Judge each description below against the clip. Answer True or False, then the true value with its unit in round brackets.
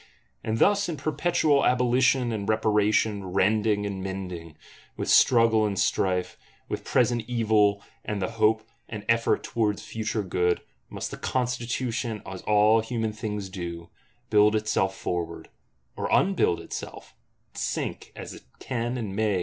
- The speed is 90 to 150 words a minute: True (140 wpm)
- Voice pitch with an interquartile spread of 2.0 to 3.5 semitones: True (3.0 semitones)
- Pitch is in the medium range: False (110 Hz)